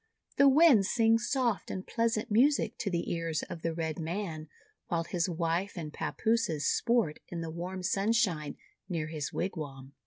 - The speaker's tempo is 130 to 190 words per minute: Yes, average, 160 wpm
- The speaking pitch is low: No, medium, 180 Hz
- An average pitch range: No, wide, 5.7 semitones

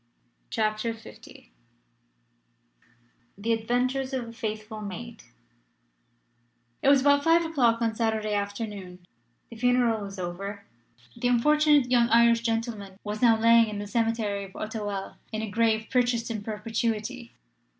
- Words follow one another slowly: Yes, slow, 130 wpm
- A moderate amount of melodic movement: No, narrow, 2.3 semitones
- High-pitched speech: Yes, high, 225 Hz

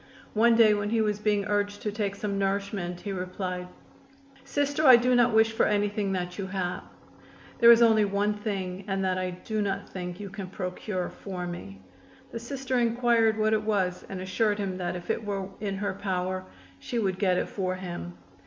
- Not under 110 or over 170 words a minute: No, average, 200 wpm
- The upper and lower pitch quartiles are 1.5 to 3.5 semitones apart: Yes, average, 2.8 semitones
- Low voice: No, high, 200 Hz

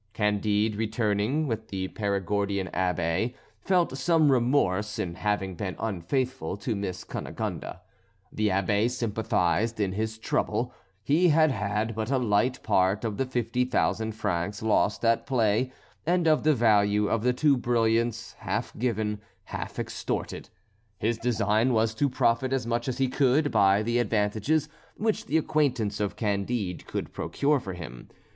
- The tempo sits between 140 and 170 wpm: Yes, average, 150 wpm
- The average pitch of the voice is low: Yes, low, 110 Hz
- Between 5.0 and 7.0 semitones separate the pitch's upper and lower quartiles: No, average, 3.7 semitones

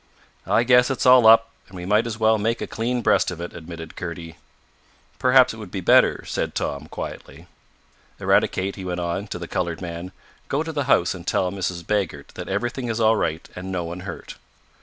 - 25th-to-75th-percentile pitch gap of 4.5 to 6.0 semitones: Yes, average, 4.8 semitones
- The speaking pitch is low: Yes, very low, 95 Hz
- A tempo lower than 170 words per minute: No, fast, 205 wpm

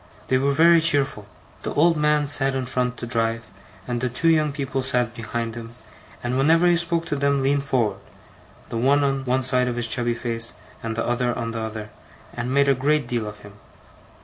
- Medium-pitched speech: No, low, 130 Hz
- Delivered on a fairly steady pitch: No, average, 3.3 semitones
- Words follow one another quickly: Yes, fast, 210 wpm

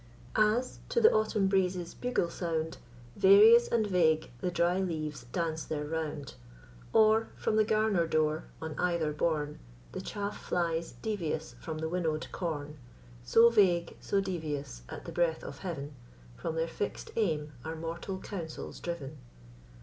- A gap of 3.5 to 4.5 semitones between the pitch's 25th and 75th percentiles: Yes, average, 4.0 semitones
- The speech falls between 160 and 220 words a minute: No, average, 150 wpm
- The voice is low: No, medium, 170 Hz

